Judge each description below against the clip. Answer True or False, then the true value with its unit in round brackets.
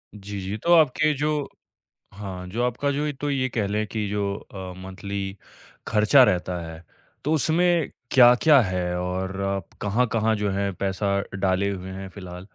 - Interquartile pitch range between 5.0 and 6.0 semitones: True (5.3 semitones)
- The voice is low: True (105 Hz)